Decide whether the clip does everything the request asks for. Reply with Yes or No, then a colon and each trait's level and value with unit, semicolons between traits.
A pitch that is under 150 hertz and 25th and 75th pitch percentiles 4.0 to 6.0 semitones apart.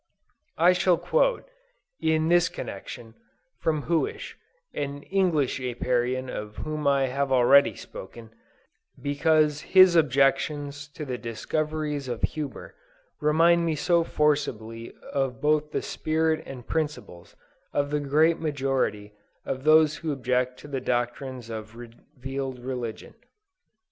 No: medium, 140 Hz; average, 3.6 semitones